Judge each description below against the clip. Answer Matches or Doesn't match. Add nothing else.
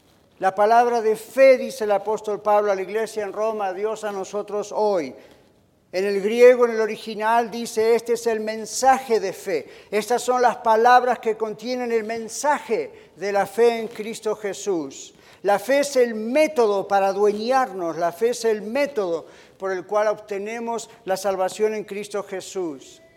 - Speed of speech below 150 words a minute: Doesn't match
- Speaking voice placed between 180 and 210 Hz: Doesn't match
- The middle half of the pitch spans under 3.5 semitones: Matches